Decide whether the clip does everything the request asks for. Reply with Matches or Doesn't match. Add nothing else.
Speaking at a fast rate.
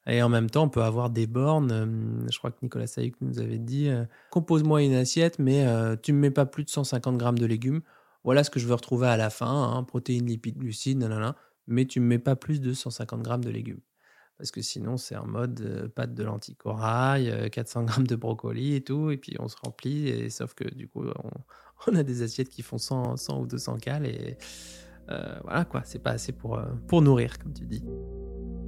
Matches